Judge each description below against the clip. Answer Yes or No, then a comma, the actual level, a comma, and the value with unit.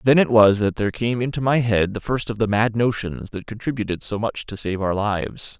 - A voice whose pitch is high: No, low, 110 Hz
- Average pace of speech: No, fast, 245 wpm